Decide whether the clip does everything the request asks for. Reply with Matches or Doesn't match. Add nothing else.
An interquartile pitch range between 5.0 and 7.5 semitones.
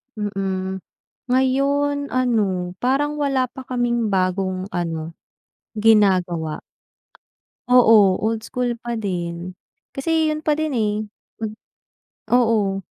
Matches